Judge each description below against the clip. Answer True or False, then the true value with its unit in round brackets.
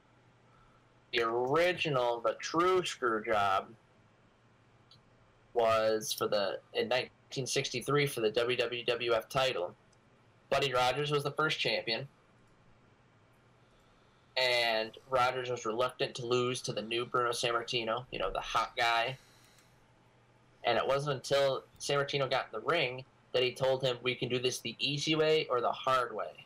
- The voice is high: False (125 Hz)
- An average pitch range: False (2.1 semitones)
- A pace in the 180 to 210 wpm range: False (135 wpm)